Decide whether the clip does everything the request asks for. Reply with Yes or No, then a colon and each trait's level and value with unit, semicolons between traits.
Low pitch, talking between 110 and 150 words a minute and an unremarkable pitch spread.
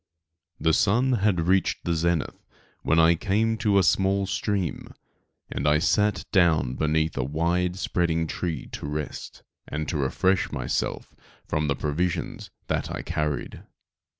Yes: very low, 85 Hz; average, 140 wpm; average, 4.0 semitones